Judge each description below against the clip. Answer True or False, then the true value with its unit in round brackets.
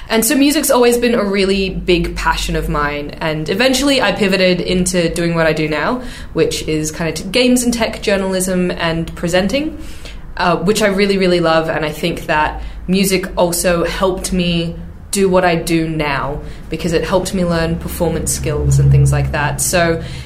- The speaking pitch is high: False (175 Hz)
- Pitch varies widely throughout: False (3.3 semitones)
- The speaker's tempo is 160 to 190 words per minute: True (185 wpm)